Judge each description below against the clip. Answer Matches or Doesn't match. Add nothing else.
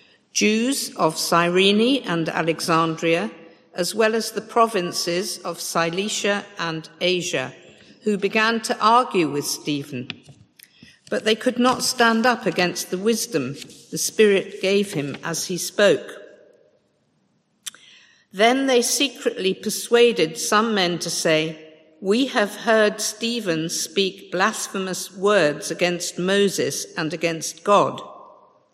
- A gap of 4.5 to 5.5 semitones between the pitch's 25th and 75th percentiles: Matches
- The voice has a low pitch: Doesn't match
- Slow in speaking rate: Matches